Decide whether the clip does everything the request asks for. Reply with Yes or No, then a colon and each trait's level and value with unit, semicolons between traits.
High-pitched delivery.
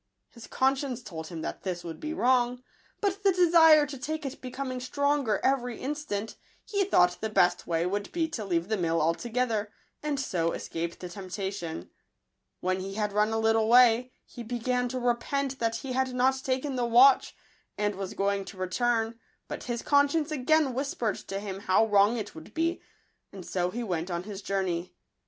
Yes: high, 235 Hz